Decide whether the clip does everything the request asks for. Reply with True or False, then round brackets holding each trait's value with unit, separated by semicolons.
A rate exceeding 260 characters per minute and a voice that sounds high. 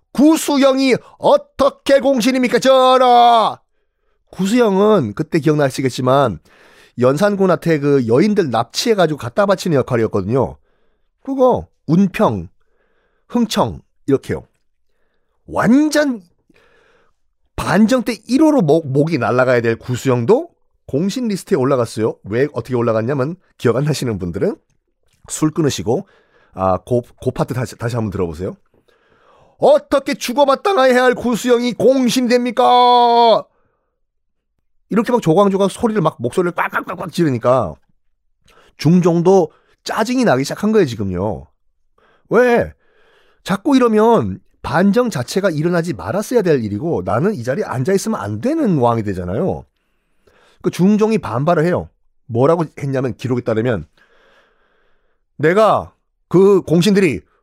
True (280 characters per minute; 195 Hz)